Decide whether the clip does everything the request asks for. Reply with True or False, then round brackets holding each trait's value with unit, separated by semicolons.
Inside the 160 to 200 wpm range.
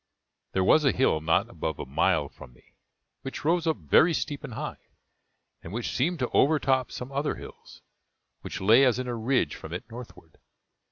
True (185 wpm)